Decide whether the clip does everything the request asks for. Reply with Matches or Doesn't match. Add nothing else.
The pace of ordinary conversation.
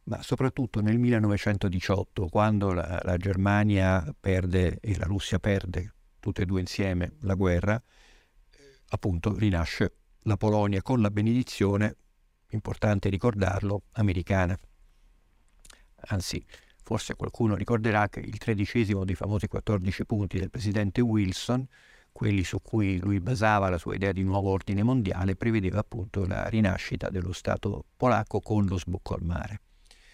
Matches